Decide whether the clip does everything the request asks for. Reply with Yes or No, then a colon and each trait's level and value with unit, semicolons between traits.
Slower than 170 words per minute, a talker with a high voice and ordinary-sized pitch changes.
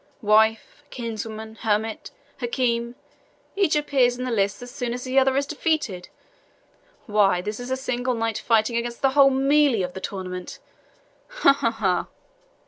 Yes: average, 155 wpm; high, 235 Hz; average, 3.5 semitones